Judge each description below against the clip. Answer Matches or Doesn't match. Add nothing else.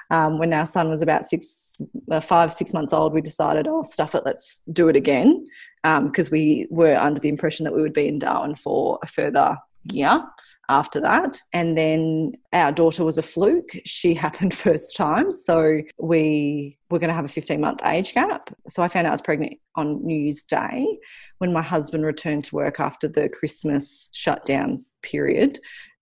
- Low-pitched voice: Doesn't match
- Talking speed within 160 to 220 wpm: Matches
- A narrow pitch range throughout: Matches